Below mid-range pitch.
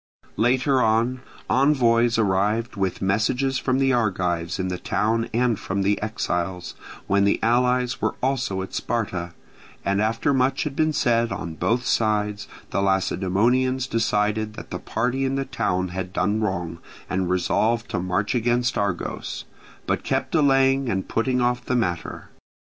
Yes: low, 110 Hz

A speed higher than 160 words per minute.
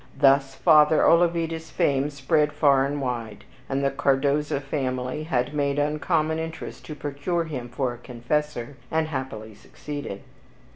No: average, 140 wpm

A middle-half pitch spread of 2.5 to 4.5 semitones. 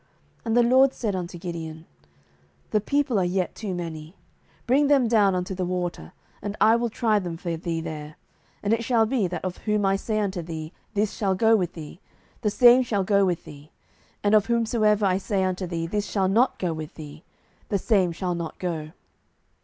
Yes: average, 4.1 semitones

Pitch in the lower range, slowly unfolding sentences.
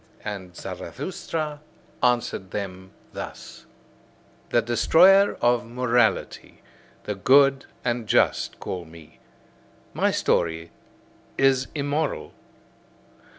Yes: low, 120 Hz; slow, 85 wpm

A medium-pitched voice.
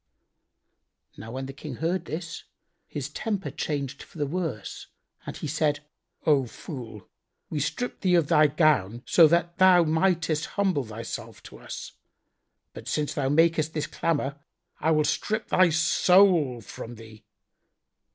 Yes: medium, 155 Hz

